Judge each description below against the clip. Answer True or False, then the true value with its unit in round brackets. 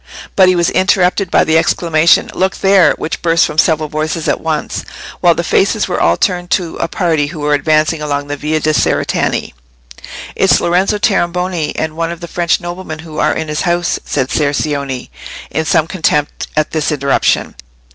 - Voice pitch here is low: False (160 Hz)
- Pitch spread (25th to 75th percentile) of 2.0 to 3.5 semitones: True (2.5 semitones)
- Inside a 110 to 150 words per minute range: False (185 wpm)